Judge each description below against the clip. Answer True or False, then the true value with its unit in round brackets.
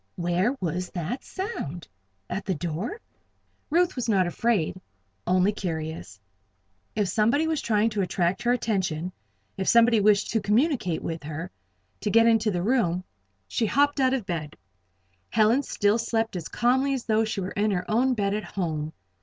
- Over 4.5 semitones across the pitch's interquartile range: True (4.9 semitones)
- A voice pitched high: True (210 Hz)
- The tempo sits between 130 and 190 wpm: True (165 wpm)